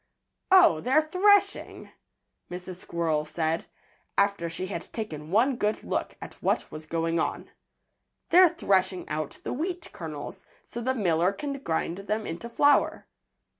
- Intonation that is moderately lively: No, wide, 7.9 semitones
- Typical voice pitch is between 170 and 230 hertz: Yes, high, 190 Hz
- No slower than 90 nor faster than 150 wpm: Yes, average, 140 wpm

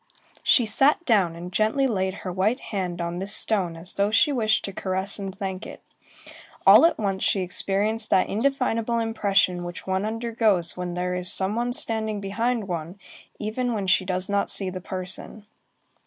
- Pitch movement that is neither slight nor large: Yes, average, 3.2 semitones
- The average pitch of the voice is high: Yes, high, 200 Hz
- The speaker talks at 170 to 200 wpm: Yes, average, 180 wpm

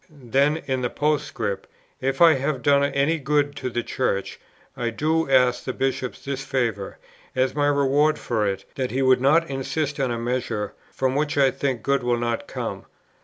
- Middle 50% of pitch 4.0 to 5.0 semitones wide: No, average, 2.7 semitones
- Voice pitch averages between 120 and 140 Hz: Yes, low, 135 Hz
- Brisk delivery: No, average, 185 wpm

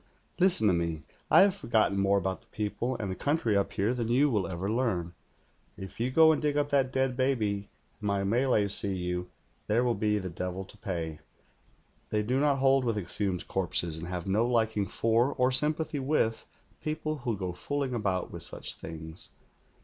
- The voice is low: Yes, low, 110 Hz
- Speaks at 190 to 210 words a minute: Yes, average, 195 wpm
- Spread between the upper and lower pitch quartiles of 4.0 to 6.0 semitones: Yes, wide, 5.5 semitones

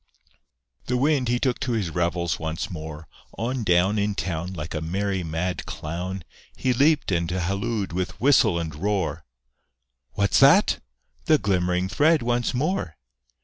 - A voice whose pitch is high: No, very low, 95 Hz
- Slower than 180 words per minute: Yes, average, 145 wpm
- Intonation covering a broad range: Yes, wide, 6.2 semitones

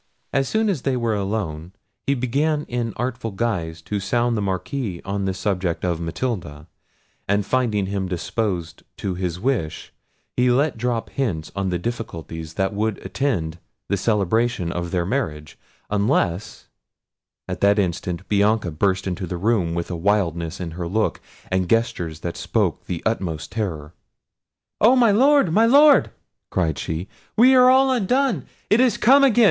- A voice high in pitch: No, low, 100 Hz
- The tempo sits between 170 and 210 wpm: No, average, 160 wpm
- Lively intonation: Yes, wide, 6.4 semitones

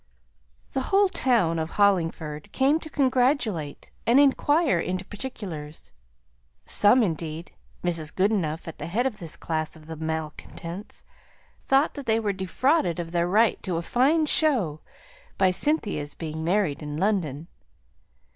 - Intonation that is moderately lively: No, wide, 7.9 semitones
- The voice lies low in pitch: No, medium, 185 Hz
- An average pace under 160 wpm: Yes, slow, 135 wpm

